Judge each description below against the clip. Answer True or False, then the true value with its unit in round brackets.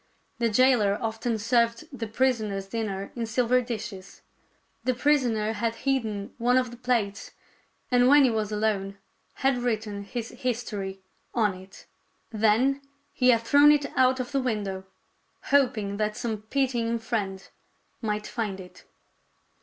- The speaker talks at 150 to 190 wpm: False (140 wpm)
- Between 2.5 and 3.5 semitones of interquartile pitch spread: True (3.2 semitones)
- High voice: True (230 Hz)